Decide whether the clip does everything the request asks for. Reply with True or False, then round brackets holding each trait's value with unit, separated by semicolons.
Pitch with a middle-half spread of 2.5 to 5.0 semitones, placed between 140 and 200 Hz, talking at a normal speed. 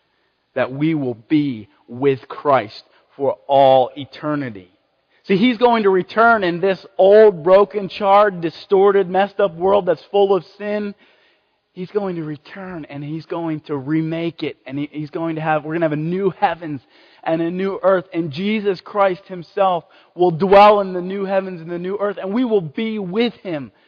True (4.3 semitones; 185 Hz; 185 wpm)